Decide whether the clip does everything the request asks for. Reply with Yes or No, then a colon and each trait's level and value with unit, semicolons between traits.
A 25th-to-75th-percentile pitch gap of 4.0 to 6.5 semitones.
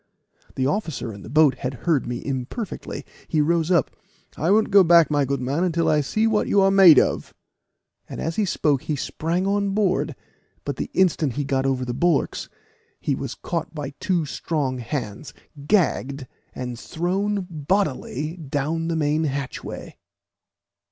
Yes: average, 4.8 semitones